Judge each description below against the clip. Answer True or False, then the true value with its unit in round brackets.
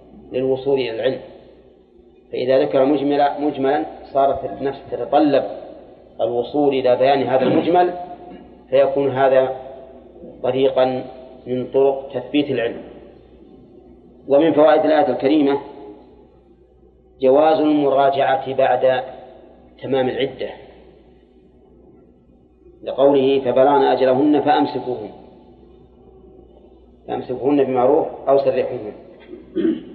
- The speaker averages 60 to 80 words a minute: True (75 wpm)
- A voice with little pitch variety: True (2.1 semitones)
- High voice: False (135 Hz)